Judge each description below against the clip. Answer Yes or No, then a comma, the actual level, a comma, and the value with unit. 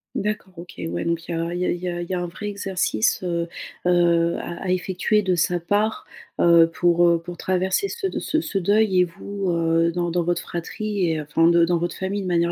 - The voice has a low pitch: No, medium, 175 Hz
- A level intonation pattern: Yes, narrow, 2.0 semitones